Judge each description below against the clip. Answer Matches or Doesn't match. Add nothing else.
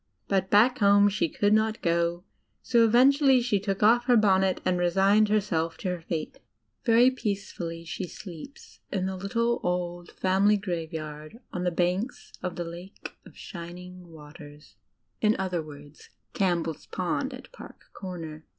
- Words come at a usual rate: Matches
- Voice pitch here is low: Doesn't match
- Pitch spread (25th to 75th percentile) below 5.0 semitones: Matches